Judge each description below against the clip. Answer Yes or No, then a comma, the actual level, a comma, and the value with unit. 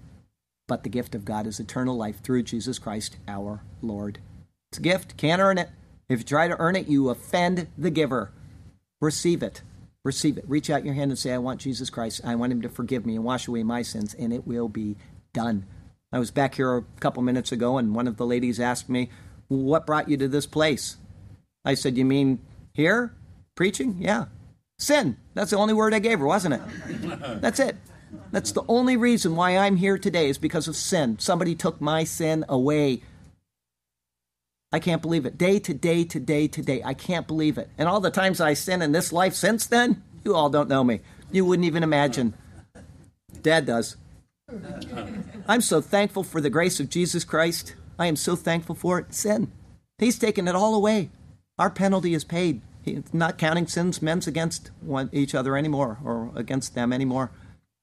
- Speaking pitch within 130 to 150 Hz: Yes, medium, 140 Hz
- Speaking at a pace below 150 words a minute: No, average, 200 wpm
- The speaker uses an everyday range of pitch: No, wide, 6.5 semitones